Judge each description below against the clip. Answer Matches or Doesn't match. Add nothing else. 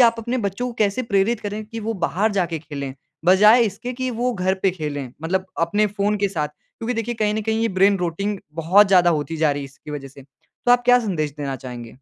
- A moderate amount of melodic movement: Doesn't match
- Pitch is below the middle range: Doesn't match